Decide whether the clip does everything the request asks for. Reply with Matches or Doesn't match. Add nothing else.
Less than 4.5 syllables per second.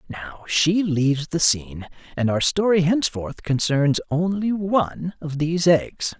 Matches